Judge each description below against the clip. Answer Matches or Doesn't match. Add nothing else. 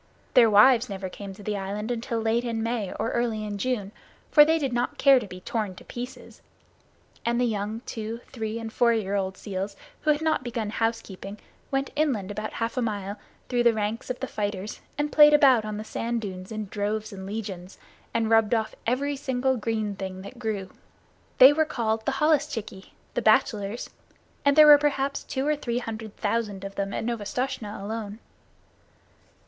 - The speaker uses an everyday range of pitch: Matches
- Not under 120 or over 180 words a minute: Doesn't match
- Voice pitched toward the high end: Matches